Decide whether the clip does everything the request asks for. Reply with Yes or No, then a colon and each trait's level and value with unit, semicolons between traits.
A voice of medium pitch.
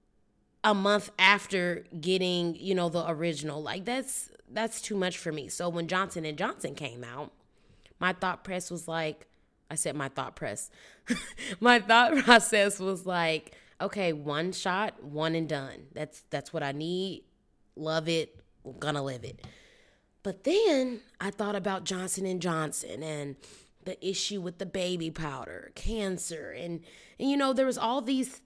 Yes: medium, 180 Hz